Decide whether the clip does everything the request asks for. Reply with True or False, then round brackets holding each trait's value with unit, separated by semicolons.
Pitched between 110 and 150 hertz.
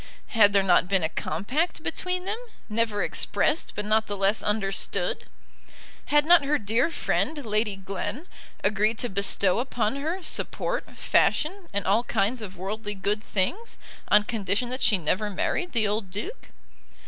False (215 Hz)